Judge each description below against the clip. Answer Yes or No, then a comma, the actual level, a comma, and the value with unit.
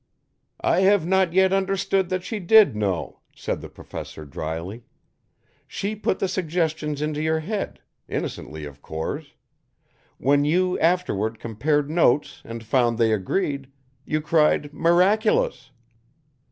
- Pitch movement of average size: No, wide, 8.1 semitones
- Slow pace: Yes, slow, 125 wpm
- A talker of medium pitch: Yes, medium, 155 Hz